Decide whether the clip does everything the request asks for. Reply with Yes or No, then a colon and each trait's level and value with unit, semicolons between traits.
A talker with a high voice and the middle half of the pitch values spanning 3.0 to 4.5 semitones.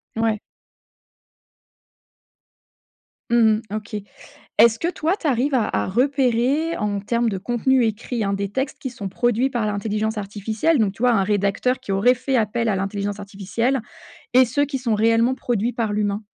Yes: high, 225 Hz; average, 3.4 semitones